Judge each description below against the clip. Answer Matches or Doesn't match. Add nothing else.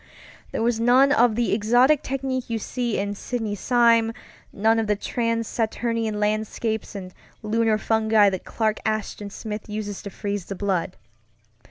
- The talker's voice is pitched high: Matches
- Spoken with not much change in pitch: Matches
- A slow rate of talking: Doesn't match